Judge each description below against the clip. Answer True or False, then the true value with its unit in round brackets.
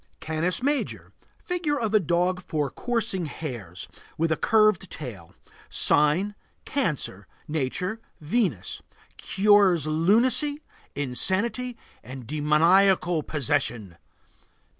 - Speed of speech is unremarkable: False (95 wpm)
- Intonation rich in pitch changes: True (6.3 semitones)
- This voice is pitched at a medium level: True (175 Hz)